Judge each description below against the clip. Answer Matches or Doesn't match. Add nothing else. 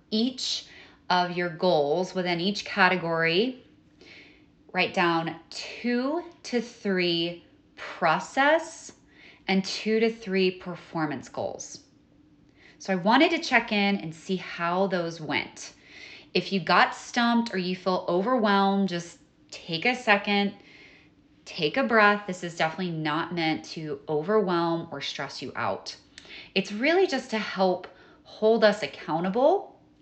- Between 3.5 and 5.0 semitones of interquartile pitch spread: Matches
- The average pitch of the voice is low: Doesn't match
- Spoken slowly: Matches